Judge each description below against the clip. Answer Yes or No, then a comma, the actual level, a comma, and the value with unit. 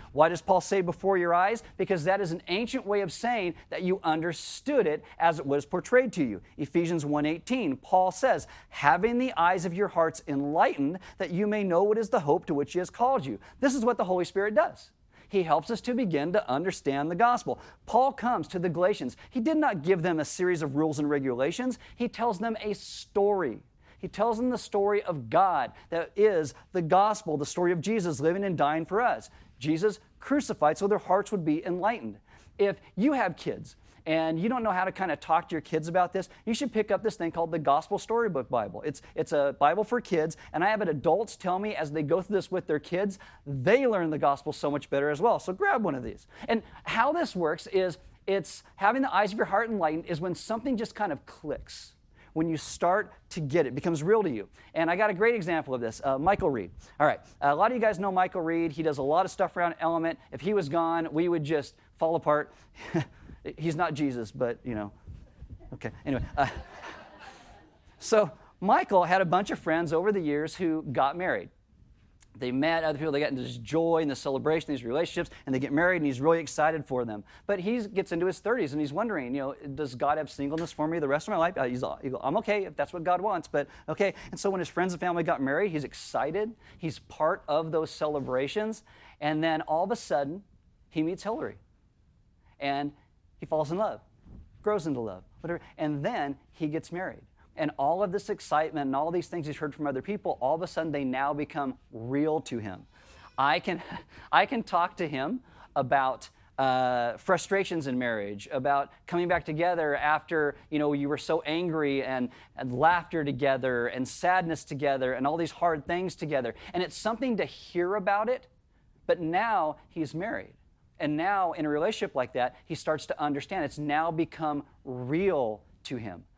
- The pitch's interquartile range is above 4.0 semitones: Yes, average, 5.2 semitones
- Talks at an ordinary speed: No, fast, 215 wpm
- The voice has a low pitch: No, medium, 165 Hz